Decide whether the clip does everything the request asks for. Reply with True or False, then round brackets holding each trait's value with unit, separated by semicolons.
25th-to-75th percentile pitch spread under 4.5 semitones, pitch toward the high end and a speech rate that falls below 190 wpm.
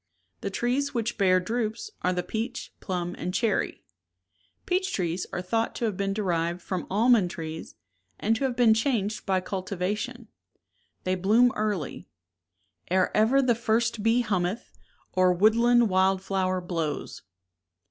True (4.1 semitones; 205 Hz; 160 wpm)